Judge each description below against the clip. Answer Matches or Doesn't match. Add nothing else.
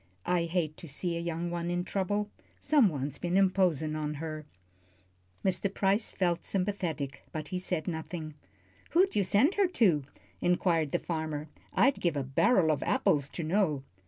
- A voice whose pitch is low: Doesn't match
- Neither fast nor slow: Matches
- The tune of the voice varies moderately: Matches